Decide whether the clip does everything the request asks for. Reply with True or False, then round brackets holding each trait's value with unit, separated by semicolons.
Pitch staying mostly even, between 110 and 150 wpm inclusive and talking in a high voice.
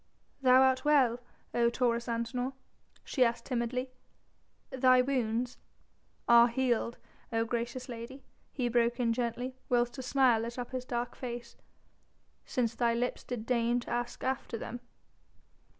True (1.4 semitones; 140 wpm; 240 Hz)